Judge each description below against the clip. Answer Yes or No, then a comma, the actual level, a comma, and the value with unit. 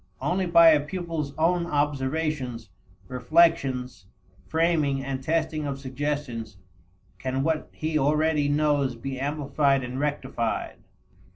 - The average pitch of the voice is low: No, medium, 145 Hz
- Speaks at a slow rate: Yes, slow, 110 wpm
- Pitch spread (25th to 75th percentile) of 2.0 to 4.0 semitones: Yes, average, 3.1 semitones